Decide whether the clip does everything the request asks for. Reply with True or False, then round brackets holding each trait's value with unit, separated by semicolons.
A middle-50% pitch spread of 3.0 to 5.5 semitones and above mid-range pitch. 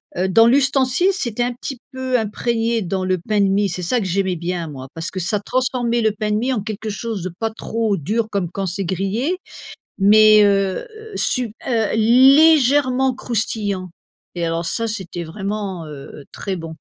True (4.3 semitones; 215 Hz)